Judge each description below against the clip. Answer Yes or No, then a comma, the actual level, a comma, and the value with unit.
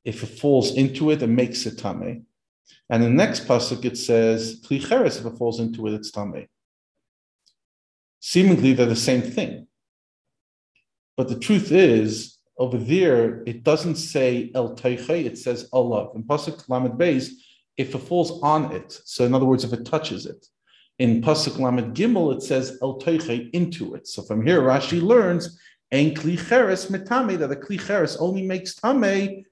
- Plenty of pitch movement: Yes, wide, 6.1 semitones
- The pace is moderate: Yes, average, 165 wpm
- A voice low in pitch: Yes, low, 130 Hz